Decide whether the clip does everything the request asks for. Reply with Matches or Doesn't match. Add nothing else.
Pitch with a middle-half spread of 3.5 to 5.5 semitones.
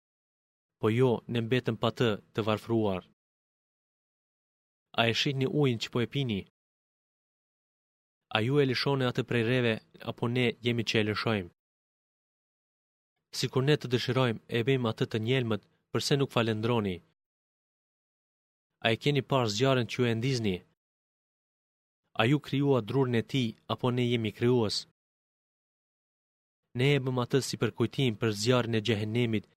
Doesn't match